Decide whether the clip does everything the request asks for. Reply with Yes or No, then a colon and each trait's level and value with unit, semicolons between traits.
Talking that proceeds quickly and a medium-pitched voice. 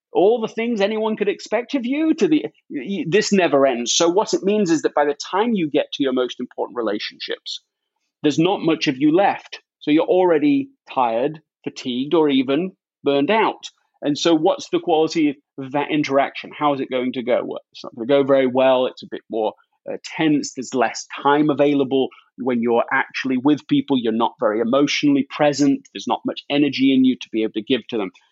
Yes: fast, 210 wpm; medium, 145 Hz